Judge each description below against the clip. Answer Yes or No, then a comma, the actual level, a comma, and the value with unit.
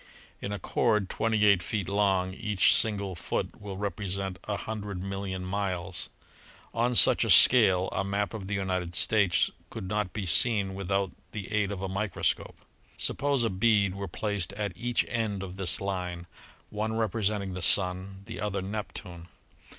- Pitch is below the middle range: Yes, low, 100 Hz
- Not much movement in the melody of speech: Yes, narrow, 2.0 semitones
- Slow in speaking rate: No, average, 165 wpm